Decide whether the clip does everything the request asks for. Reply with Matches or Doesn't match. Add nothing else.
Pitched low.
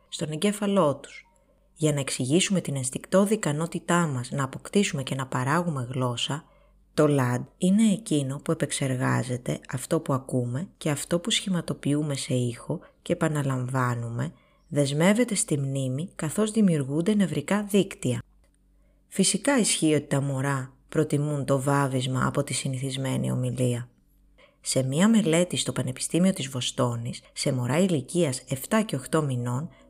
Doesn't match